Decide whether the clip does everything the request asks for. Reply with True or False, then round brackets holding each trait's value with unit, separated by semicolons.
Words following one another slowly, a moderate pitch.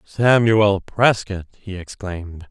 False (95 wpm; 100 Hz)